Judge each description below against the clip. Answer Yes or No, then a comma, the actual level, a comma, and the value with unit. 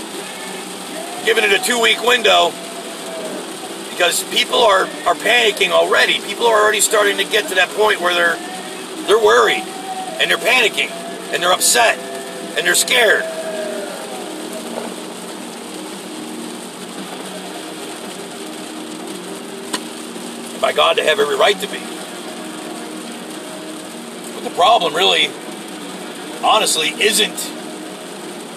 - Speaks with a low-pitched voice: No, very high, 375 Hz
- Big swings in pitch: Yes, wide, 8.7 semitones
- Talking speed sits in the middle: No, slow, 100 wpm